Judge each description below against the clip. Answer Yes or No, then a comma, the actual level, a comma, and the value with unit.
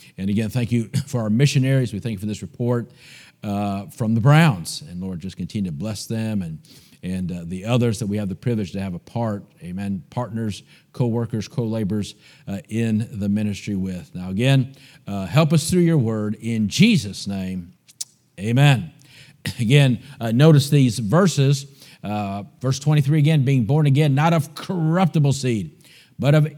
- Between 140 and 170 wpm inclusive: Yes, average, 165 wpm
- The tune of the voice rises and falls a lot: Yes, wide, 5.8 semitones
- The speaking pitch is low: Yes, low, 120 Hz